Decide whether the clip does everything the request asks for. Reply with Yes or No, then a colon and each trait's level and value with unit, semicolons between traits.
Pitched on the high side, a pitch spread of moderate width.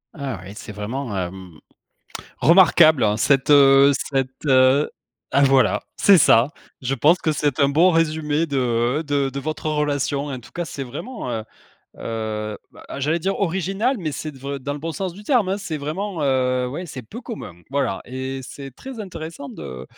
No: medium, 140 Hz; average, 4.0 semitones